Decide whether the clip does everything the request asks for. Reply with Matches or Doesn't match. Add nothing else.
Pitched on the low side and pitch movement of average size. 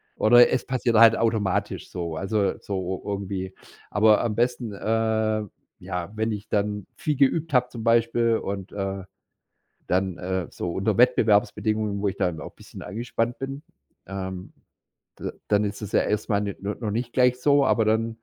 Matches